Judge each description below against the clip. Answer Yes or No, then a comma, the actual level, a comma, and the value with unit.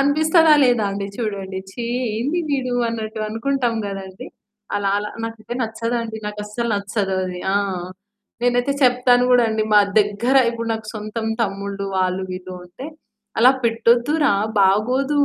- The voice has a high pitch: Yes, high, 225 Hz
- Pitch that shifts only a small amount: No, average, 3.5 semitones